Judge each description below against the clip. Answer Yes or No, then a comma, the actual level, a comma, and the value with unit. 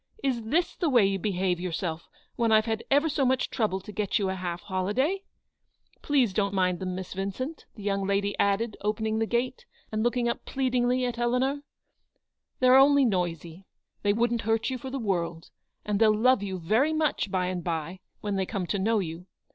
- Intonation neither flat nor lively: Yes, average, 4.9 semitones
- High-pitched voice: Yes, high, 215 Hz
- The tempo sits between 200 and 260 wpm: Yes, fast, 205 wpm